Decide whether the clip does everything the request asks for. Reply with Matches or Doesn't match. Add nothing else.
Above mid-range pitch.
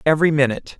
Doesn't match